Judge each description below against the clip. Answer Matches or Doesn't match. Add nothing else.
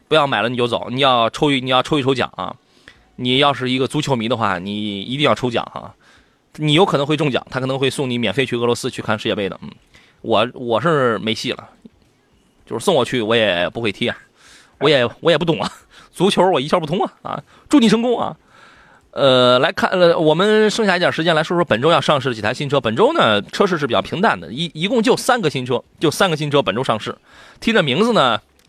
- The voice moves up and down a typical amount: Matches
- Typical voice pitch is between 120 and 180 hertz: Matches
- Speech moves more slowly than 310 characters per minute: Doesn't match